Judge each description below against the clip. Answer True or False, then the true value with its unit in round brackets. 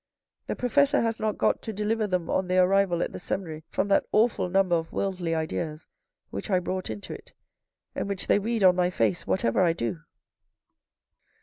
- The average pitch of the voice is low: False (185 Hz)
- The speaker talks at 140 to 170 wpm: False (190 wpm)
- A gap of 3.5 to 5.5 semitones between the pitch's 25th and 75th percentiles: True (3.8 semitones)